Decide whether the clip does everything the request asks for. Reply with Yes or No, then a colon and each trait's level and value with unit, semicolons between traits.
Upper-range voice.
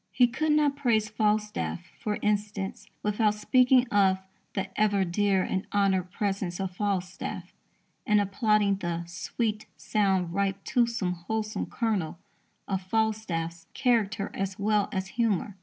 Yes: high, 205 Hz